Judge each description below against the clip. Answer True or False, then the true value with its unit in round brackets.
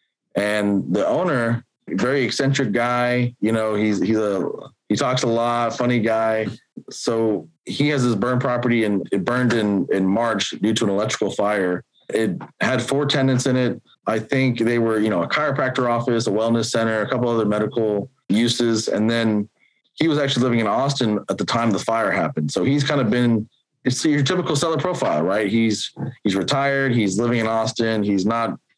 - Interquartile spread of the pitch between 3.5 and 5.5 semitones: False (2.9 semitones)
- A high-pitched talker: False (115 Hz)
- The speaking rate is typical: True (190 wpm)